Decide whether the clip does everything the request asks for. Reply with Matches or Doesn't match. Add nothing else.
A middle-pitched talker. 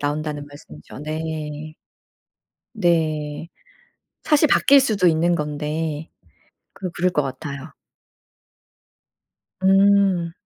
Matches